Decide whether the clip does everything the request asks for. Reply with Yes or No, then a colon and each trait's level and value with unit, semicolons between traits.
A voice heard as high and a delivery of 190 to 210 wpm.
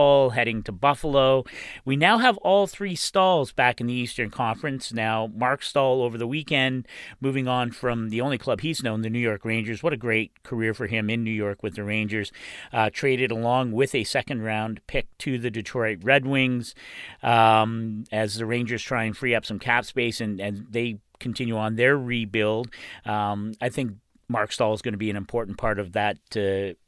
No: low, 115 Hz; average, 200 wpm